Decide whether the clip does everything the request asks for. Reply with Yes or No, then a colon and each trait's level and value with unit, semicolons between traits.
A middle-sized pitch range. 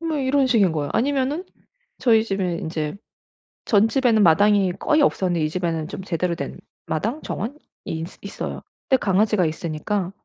No: wide, 6.2 semitones